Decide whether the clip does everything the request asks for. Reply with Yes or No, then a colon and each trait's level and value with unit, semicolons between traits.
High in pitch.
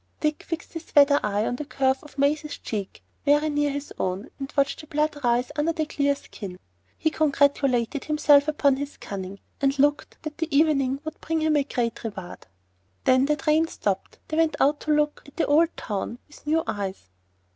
Yes: very high, 285 Hz